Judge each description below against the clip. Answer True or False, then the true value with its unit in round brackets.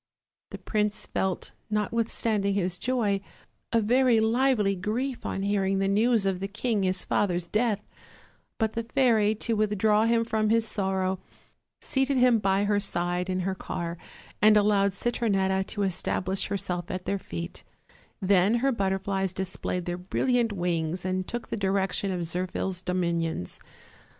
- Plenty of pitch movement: False (3.0 semitones)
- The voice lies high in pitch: True (200 Hz)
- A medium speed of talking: True (150 wpm)